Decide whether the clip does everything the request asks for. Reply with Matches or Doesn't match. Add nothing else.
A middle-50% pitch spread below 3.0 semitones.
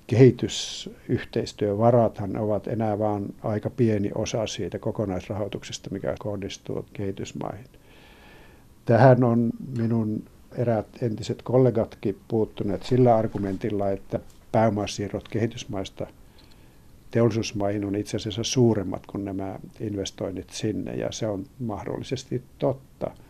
Matches